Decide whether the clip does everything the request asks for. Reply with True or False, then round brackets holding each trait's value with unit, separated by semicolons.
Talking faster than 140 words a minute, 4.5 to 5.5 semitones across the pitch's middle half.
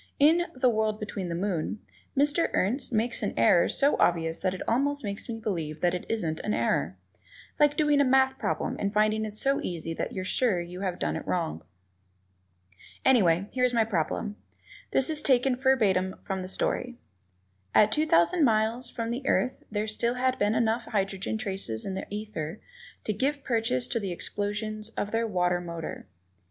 True (185 wpm; 5.2 semitones)